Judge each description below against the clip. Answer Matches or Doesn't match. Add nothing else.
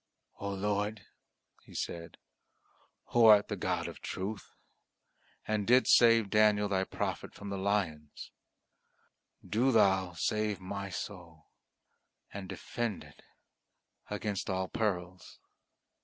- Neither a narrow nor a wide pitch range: Doesn't match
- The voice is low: Matches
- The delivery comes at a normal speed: Doesn't match